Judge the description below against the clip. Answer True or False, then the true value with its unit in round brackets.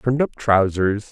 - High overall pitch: False (110 Hz)